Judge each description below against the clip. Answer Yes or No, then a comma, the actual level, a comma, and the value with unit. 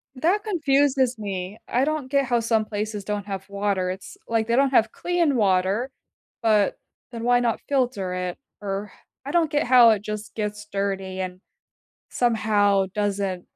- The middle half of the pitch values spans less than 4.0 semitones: No, average, 4.4 semitones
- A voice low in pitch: No, high, 215 Hz